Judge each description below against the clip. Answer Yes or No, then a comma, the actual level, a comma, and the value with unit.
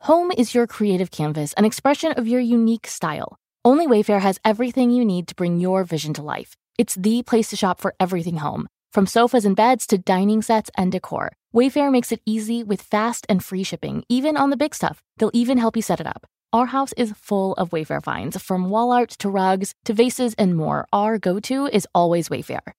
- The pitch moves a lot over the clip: No, average, 4.3 semitones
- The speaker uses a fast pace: Yes, fast, 220 wpm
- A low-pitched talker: No, high, 215 Hz